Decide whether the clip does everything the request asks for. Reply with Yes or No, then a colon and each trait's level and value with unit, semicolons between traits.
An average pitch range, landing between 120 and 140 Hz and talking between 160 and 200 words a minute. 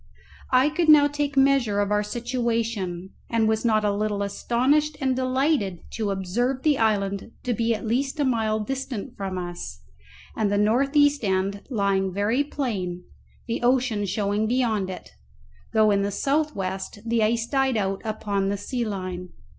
No: average, 4.5 semitones; high, 220 Hz; average, 170 wpm